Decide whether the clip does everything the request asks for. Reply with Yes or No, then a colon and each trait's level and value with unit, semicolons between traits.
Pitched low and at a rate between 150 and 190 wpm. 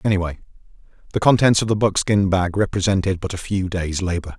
Yes: very low, 95 Hz; average, 180 wpm